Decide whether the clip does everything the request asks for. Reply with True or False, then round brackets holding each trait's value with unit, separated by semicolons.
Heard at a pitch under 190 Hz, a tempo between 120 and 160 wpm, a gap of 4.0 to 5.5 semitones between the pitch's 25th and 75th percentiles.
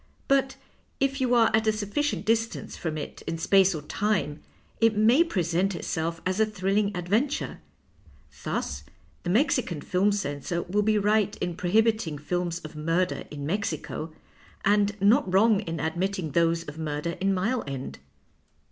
False (195 Hz; 155 wpm; 4.6 semitones)